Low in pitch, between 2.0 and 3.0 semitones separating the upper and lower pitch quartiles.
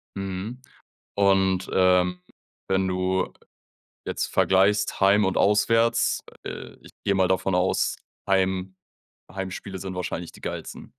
No: very low, 95 Hz; narrow, 1.1 semitones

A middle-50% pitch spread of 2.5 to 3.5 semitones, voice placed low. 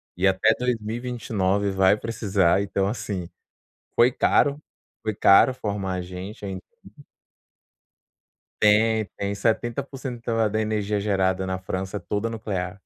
Yes: average, 2.8 semitones; low, 100 Hz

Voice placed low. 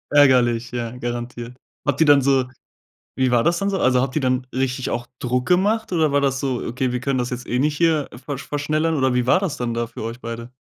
Yes: low, 130 Hz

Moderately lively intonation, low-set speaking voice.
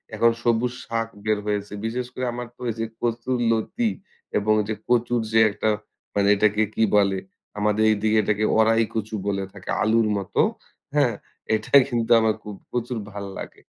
No: narrow, 2.0 semitones; low, 110 Hz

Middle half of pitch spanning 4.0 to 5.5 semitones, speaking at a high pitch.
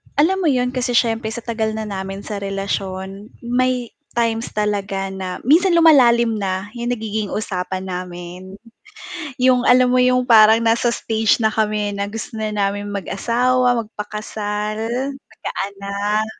No: average, 3.3 semitones; high, 220 Hz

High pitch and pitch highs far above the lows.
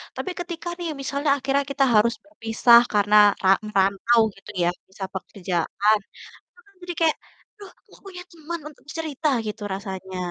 Yes: high, 240 Hz; wide, 8.3 semitones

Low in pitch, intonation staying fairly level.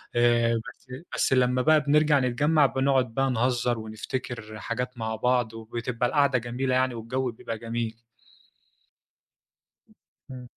Yes: low, 125 Hz; narrow, 2.1 semitones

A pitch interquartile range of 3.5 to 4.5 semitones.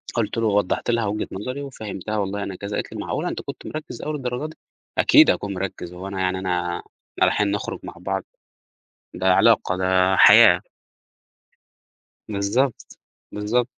Yes: average, 3.9 semitones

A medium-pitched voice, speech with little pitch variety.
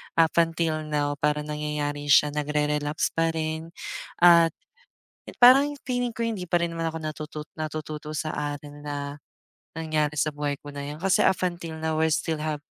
Yes: medium, 155 Hz; narrow, 1.9 semitones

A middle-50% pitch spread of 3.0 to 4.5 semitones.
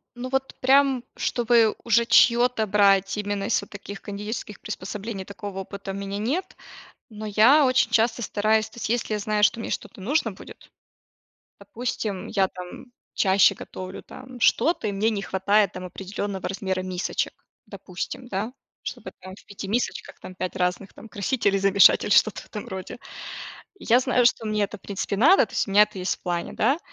Yes: average, 3.3 semitones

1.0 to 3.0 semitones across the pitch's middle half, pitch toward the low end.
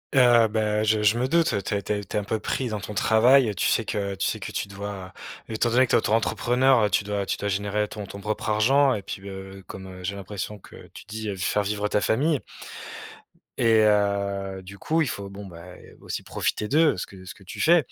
Yes: narrow, 2.4 semitones; low, 105 Hz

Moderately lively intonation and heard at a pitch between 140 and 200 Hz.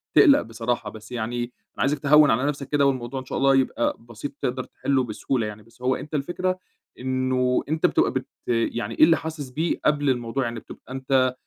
No: average, 3.2 semitones; low, 130 Hz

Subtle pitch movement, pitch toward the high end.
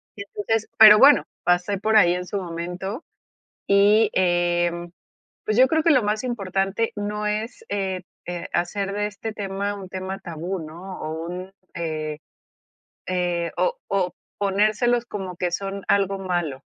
No: average, 3.0 semitones; high, 195 Hz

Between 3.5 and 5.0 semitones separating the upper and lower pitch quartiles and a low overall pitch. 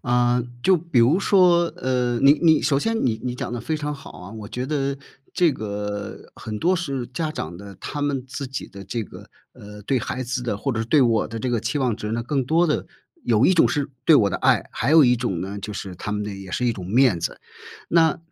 No: wide, 5.4 semitones; low, 125 Hz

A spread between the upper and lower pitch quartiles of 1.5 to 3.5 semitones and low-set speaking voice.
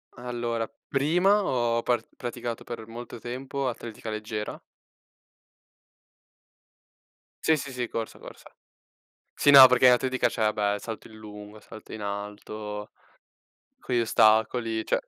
Yes: narrow, 2.6 semitones; low, 115 Hz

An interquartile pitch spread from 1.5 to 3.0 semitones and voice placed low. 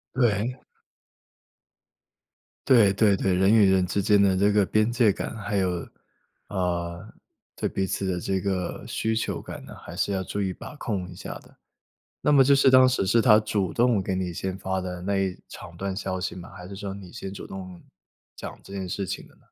Yes: narrow, 2.4 semitones; very low, 95 Hz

